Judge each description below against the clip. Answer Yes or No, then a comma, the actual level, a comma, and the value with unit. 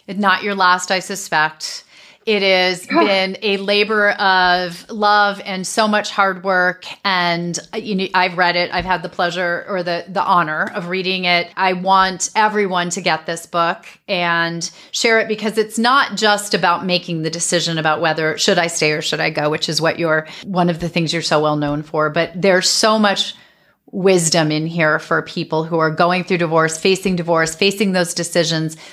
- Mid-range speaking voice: Yes, medium, 180 Hz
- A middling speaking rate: Yes, average, 190 wpm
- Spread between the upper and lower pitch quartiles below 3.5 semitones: Yes, average, 2.8 semitones